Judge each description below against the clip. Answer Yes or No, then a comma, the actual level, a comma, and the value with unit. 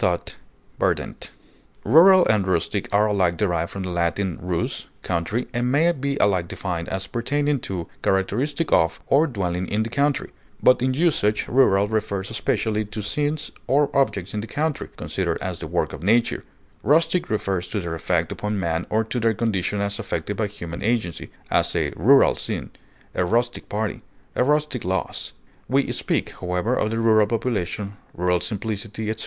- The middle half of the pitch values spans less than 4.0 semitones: No, average, 5.1 semitones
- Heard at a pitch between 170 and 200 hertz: No, low, 105 Hz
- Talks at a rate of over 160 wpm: Yes, average, 170 wpm